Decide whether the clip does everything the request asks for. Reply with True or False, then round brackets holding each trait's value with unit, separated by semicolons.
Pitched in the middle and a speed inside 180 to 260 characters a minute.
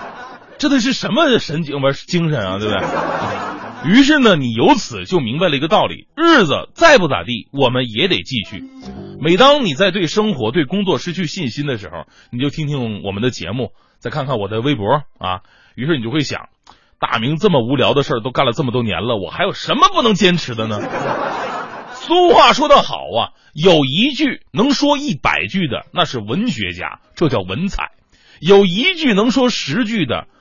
False (155 Hz; 275 characters per minute)